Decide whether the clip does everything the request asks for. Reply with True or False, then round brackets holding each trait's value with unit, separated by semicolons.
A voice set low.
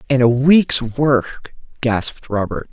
True (125 Hz)